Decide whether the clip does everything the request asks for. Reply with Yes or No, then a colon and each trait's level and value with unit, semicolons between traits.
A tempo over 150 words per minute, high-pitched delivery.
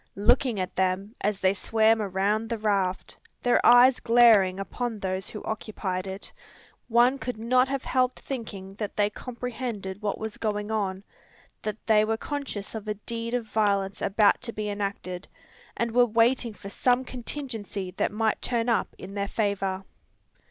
Yes: average, 165 wpm; high, 215 Hz